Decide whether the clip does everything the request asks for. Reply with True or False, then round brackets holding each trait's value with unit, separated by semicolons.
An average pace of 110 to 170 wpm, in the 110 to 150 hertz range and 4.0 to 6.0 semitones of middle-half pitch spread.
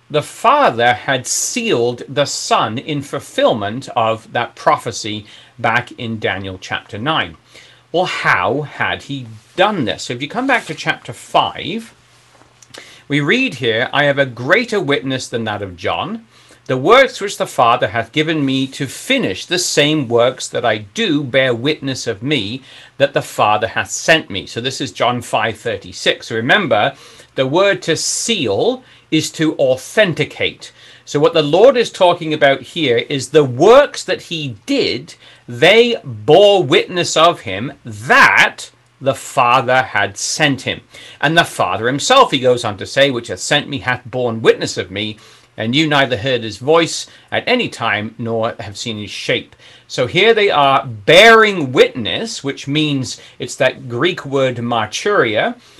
True (165 wpm; 135 Hz; 5.1 semitones)